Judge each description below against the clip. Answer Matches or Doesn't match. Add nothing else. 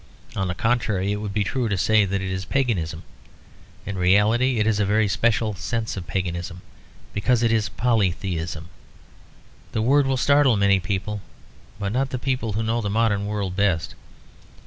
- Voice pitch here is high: Doesn't match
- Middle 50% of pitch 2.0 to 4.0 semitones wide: Matches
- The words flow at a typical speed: Matches